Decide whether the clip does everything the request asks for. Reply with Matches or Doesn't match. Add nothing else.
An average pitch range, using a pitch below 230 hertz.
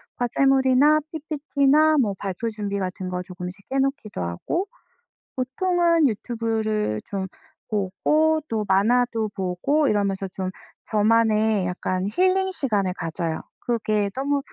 Doesn't match